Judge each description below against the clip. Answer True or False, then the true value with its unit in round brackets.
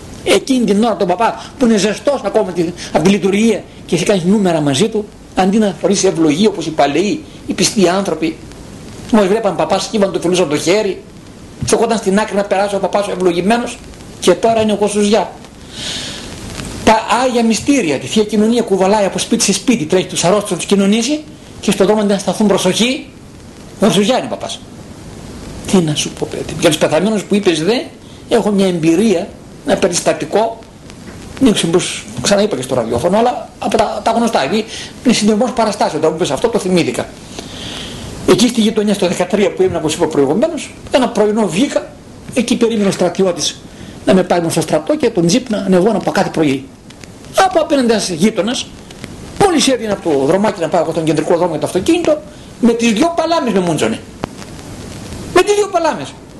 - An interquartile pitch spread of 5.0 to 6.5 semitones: False (4.1 semitones)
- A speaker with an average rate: False (185 wpm)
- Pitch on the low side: False (205 Hz)